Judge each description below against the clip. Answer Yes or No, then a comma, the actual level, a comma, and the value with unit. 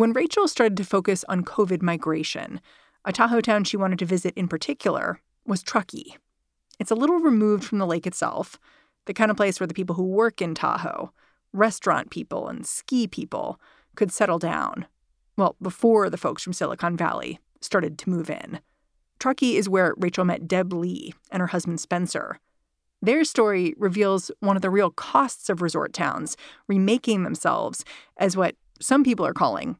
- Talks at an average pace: Yes, average, 175 wpm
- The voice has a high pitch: Yes, high, 195 Hz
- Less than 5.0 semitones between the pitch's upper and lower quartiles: Yes, average, 3.6 semitones